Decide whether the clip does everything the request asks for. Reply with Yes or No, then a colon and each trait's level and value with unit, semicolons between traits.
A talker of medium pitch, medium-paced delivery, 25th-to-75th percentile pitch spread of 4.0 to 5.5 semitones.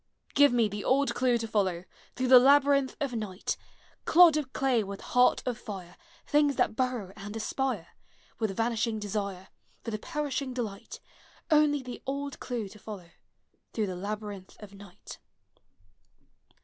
No: high, 230 Hz; average, 160 wpm; average, 4.7 semitones